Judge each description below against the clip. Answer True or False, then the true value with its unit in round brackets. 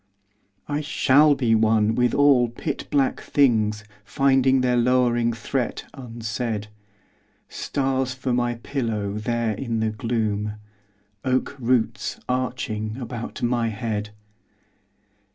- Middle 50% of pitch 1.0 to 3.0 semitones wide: True (2.7 semitones)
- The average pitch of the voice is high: False (120 Hz)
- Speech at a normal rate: False (110 wpm)